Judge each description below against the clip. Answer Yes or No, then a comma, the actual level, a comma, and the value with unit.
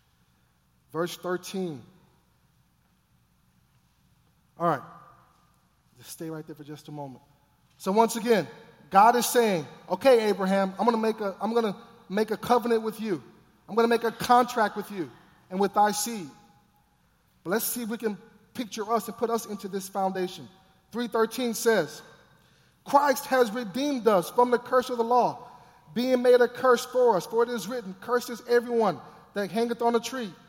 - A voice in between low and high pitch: No, high, 220 Hz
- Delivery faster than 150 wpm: Yes, average, 165 wpm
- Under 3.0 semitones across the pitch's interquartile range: No, average, 4.6 semitones